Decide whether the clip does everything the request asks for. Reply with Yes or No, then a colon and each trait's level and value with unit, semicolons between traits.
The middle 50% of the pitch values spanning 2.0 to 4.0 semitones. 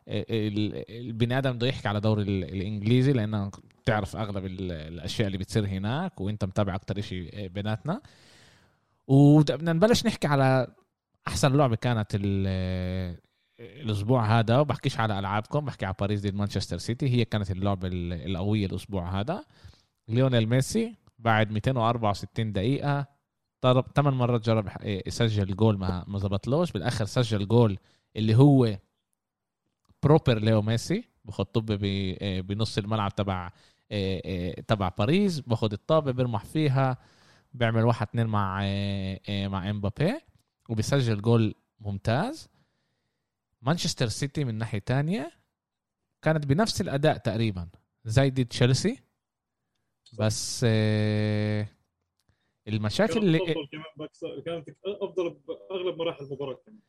No: average, 4.9 semitones